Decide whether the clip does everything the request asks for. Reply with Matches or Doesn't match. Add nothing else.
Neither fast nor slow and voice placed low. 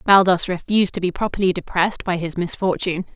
Doesn't match